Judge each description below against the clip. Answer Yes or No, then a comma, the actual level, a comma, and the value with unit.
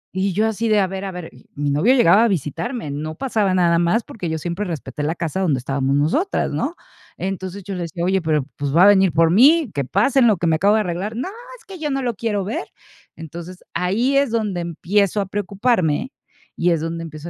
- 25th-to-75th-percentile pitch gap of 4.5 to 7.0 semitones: Yes, average, 4.8 semitones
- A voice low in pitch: No, medium, 185 Hz